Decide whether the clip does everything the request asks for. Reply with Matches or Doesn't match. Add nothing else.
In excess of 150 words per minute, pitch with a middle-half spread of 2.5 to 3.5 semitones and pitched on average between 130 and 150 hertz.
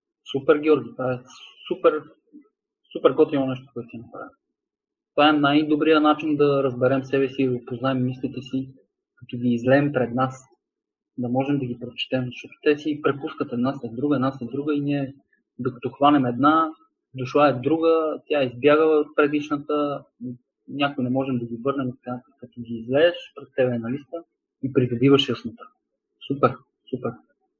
Matches